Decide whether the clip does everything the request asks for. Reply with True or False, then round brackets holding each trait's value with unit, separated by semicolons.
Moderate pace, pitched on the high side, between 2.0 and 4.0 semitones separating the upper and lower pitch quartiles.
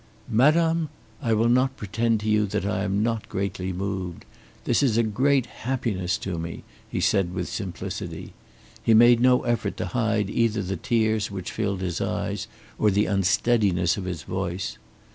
False (170 wpm; 105 Hz; 3.7 semitones)